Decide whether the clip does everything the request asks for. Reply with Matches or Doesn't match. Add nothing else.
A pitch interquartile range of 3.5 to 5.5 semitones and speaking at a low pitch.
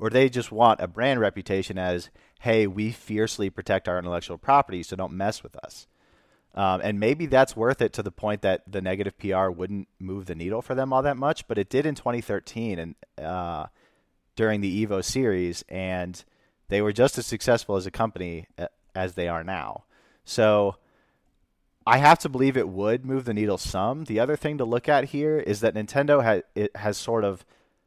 Matches